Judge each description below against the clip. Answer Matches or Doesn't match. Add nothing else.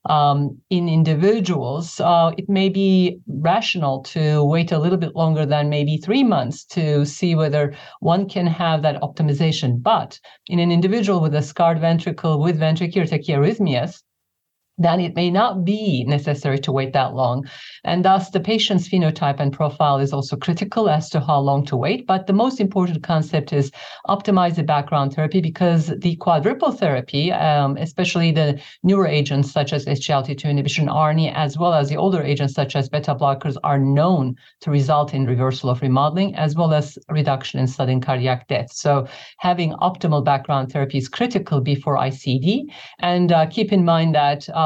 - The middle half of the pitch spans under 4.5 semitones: Matches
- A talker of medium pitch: Matches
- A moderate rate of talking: Matches